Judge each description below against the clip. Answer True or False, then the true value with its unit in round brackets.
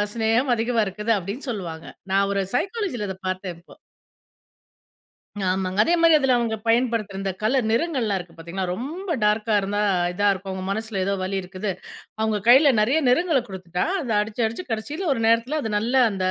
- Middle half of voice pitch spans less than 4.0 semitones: False (4.4 semitones)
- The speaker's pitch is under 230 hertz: True (220 Hz)